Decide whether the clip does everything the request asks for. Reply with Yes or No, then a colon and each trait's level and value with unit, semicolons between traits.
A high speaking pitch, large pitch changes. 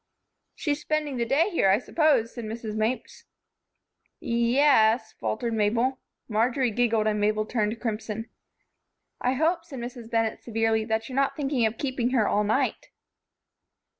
No: high, 235 Hz; average, 3.2 semitones